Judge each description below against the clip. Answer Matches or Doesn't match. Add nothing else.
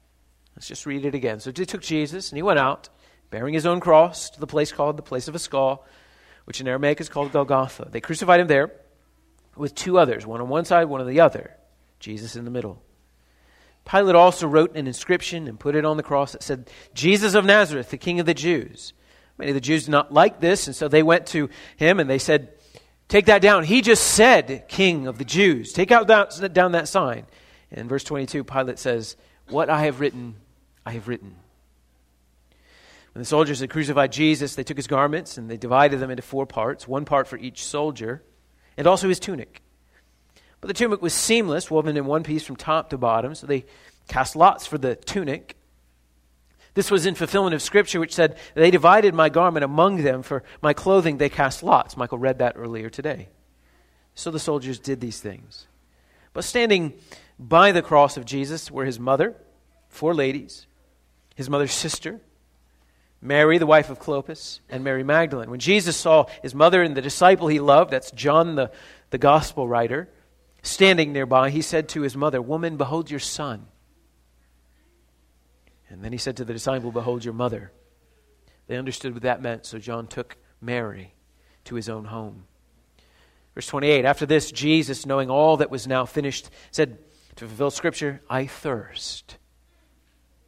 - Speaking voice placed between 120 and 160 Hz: Matches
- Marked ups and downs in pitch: Matches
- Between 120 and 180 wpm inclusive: Doesn't match